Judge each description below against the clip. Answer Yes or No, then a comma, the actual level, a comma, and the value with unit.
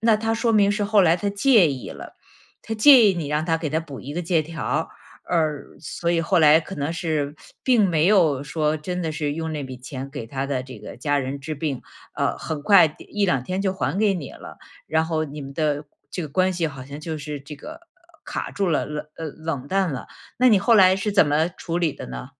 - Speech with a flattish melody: No, average, 4.5 semitones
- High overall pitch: No, medium, 160 Hz